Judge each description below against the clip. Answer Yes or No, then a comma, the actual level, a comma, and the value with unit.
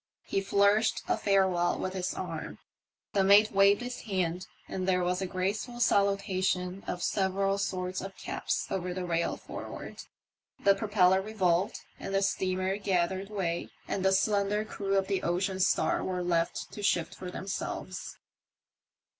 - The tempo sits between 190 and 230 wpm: No, average, 150 wpm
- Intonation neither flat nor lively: No, narrow, 1.6 semitones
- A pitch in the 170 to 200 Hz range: Yes, high, 190 Hz